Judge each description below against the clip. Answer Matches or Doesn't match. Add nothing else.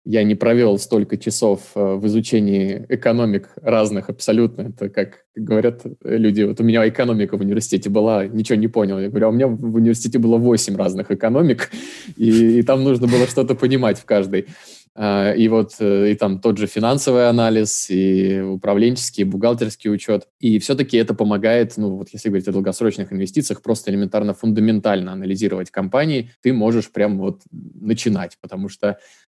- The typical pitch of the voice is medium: Doesn't match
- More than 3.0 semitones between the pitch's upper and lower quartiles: Doesn't match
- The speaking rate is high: Matches